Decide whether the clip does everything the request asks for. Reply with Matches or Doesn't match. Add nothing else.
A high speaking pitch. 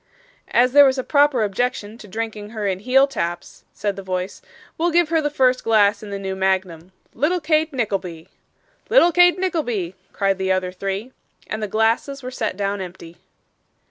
Matches